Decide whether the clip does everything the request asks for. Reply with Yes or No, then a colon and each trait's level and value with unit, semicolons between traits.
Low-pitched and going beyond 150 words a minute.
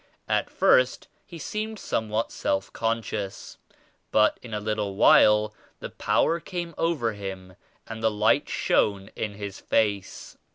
No: low, 110 Hz; slow, 135 wpm